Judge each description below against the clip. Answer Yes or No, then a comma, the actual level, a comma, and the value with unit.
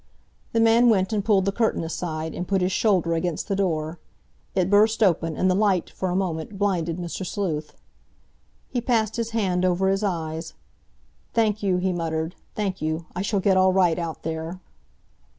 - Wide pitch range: No, average, 3.5 semitones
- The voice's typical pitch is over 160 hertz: Yes, medium, 185 Hz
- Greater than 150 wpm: Yes, average, 185 wpm